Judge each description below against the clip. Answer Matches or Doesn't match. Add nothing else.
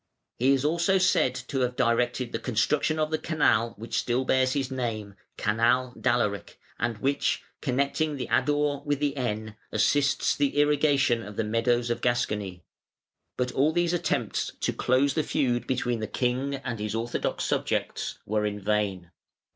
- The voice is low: Matches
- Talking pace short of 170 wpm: Matches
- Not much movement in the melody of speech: Doesn't match